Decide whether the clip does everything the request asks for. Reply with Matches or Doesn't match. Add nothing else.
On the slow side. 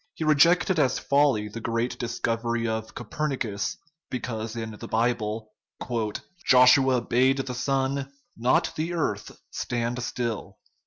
Matches